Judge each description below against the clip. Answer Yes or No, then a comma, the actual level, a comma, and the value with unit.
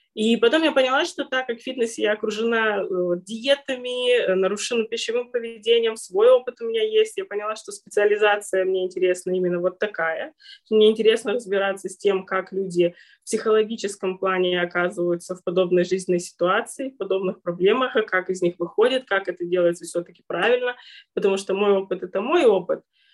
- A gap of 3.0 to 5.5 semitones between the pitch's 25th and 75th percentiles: Yes, average, 4.2 semitones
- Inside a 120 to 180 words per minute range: Yes, fast, 160 wpm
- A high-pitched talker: Yes, high, 205 Hz